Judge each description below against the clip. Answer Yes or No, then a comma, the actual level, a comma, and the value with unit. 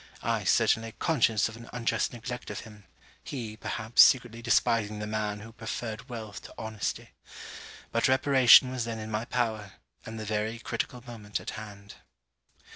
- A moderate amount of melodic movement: No, narrow, 1.8 semitones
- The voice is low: Yes, low, 115 Hz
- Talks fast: No, average, 160 wpm